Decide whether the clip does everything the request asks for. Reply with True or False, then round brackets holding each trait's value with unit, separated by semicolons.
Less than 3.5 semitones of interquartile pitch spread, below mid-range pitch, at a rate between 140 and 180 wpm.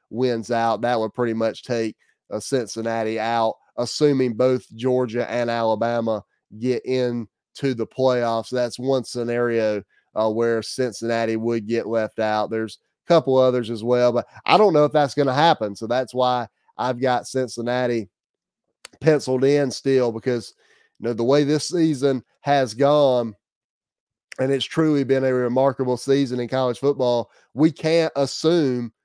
True (2.6 semitones; 125 Hz; 155 wpm)